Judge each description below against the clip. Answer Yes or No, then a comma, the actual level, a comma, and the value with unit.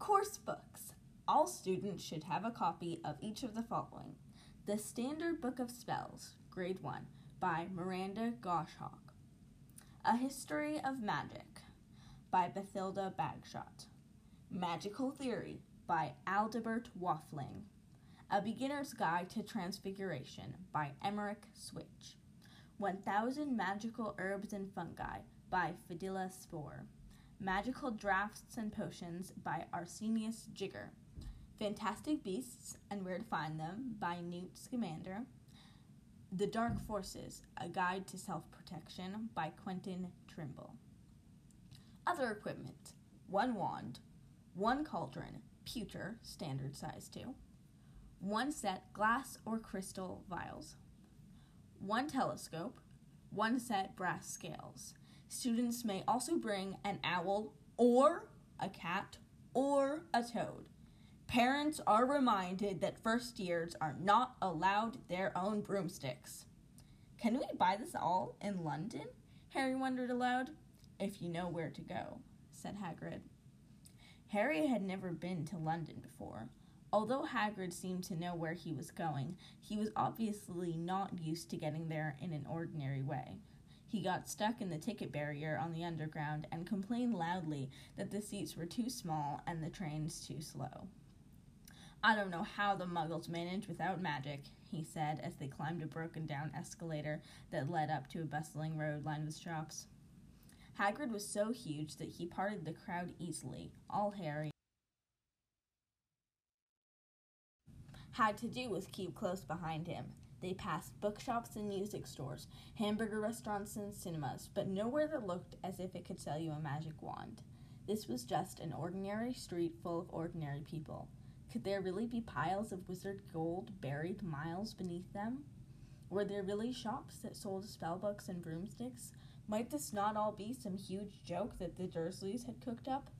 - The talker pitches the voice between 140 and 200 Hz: Yes, high, 190 Hz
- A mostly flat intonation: No, average, 4.8 semitones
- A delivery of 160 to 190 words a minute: No, average, 140 wpm